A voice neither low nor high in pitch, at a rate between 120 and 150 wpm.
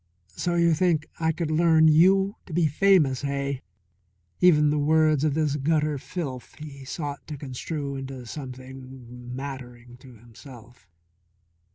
Yes: medium, 145 Hz; average, 140 wpm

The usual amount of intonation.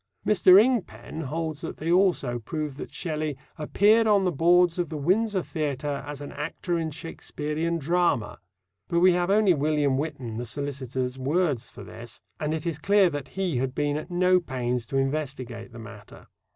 Yes: average, 4.5 semitones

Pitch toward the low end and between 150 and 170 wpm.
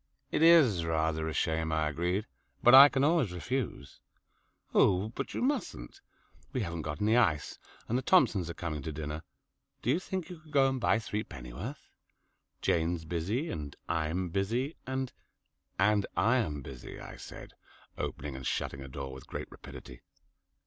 Yes: very low, 90 Hz; average, 165 wpm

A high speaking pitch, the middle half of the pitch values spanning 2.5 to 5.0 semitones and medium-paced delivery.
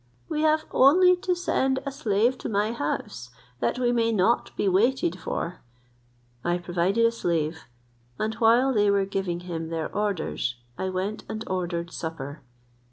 No: high, 200 Hz; wide, 5.5 semitones; average, 160 wpm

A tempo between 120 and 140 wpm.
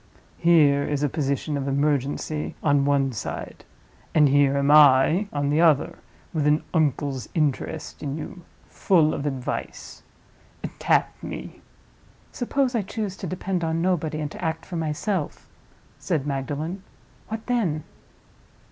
Yes: slow, 135 wpm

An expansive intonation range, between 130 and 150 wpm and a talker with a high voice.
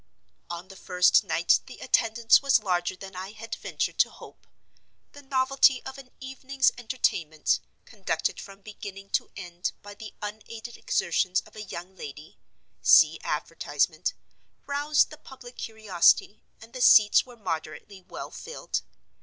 Yes: wide, 5.7 semitones; average, 145 wpm; high, 215 Hz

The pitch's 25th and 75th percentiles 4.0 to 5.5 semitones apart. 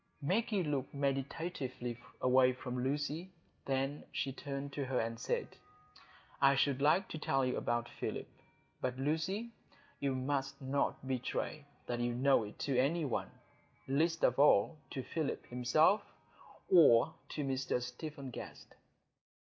No: average, 2.8 semitones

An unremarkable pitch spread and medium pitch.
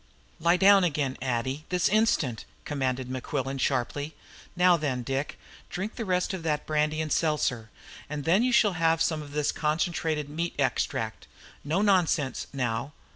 Yes: average, 4.4 semitones; medium, 150 Hz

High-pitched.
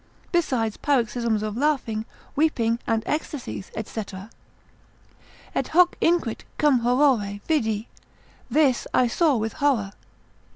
Yes: high, 245 Hz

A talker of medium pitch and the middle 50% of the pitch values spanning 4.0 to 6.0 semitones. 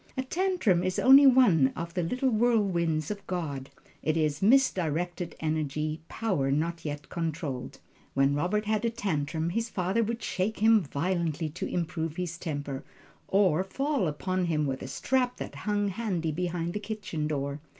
Yes: medium, 175 Hz; average, 5.3 semitones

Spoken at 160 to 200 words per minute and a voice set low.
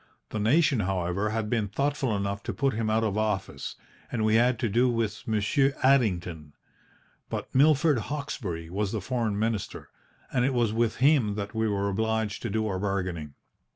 Yes: average, 180 wpm; low, 110 Hz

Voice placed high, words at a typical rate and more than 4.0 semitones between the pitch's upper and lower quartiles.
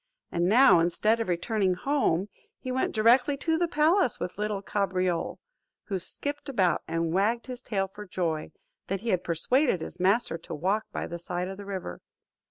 Yes: high, 200 Hz; average, 180 wpm; average, 5.3 semitones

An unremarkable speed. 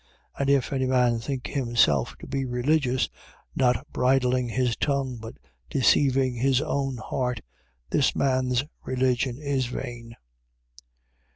No: slow, 125 wpm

